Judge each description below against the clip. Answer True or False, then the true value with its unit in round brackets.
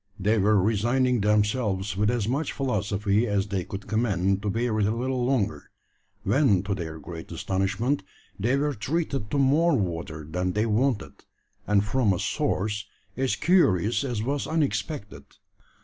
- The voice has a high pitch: False (105 Hz)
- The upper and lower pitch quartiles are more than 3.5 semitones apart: True (4.7 semitones)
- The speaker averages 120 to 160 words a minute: True (155 wpm)